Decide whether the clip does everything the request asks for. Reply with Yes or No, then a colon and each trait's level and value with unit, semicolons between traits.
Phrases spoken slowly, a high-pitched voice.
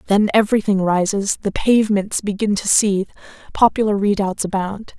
Yes: slow, 130 wpm; high, 200 Hz